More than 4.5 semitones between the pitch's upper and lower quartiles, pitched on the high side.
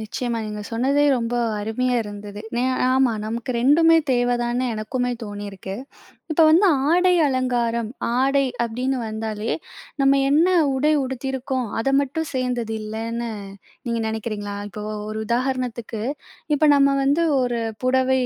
No: average, 3.3 semitones; high, 245 Hz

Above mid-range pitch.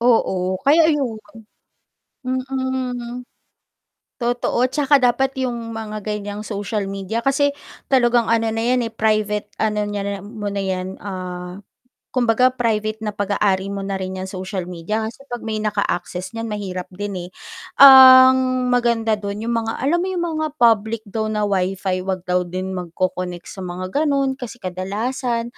Yes: high, 220 Hz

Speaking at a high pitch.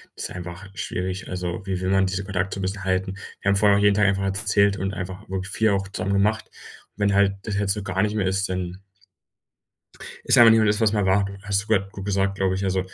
No: very low, 95 Hz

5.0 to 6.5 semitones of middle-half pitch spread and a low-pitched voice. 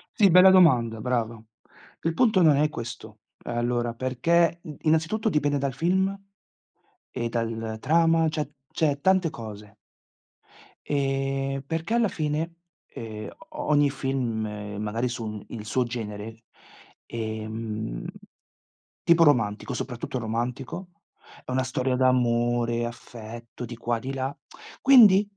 Yes: wide, 5.6 semitones; low, 130 Hz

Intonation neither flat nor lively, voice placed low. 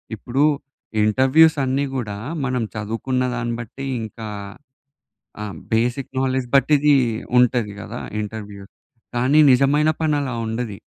Yes: average, 3.5 semitones; low, 125 Hz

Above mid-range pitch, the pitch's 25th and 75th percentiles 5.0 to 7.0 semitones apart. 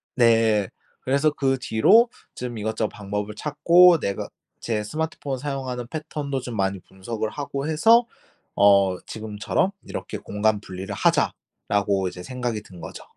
No: low, 115 Hz; wide, 5.5 semitones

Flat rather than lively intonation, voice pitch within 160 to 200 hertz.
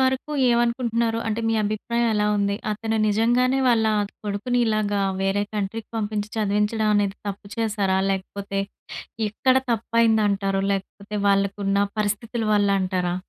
No: narrow, 2.2 semitones; high, 210 Hz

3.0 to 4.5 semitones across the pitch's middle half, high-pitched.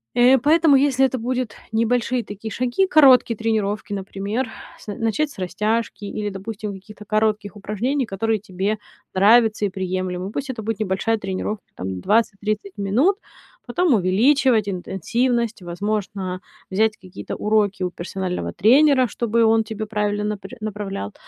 Yes: average, 3.3 semitones; high, 215 Hz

